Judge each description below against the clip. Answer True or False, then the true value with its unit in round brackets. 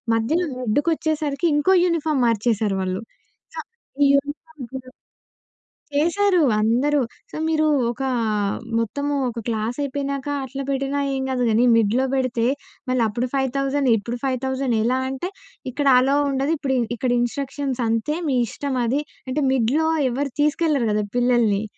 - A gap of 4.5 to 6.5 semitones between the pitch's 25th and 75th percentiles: False (3.2 semitones)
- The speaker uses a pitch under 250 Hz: False (265 Hz)